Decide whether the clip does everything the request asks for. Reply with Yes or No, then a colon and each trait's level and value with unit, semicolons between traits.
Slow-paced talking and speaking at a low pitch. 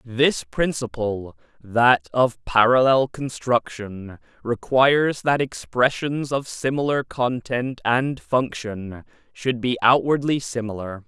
Yes: slow, 95 wpm; low, 120 Hz